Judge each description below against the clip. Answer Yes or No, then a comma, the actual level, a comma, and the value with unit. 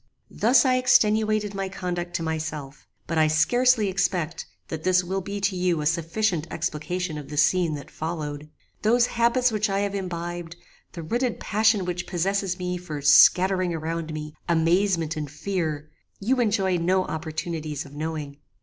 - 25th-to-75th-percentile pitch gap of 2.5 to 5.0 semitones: Yes, average, 4.1 semitones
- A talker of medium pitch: Yes, medium, 175 Hz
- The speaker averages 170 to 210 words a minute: No, average, 160 wpm